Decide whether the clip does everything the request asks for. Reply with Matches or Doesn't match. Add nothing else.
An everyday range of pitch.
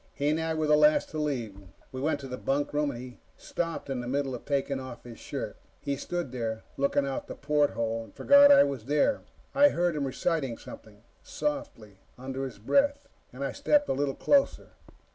Matches